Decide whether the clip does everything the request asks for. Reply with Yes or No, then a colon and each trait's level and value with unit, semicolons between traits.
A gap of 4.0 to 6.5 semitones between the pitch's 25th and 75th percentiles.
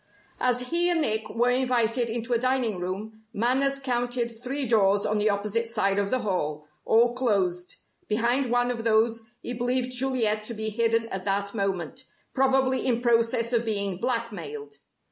No: average, 2.9 semitones